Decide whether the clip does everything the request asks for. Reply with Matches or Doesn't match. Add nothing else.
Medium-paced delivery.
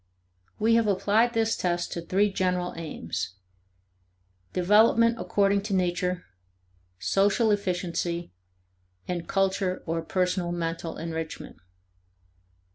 Doesn't match